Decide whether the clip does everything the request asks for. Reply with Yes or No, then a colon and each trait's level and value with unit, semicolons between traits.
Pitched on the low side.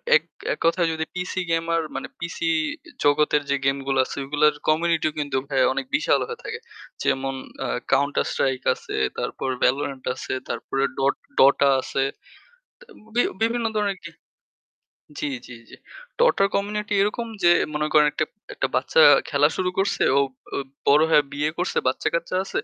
No: medium, 155 Hz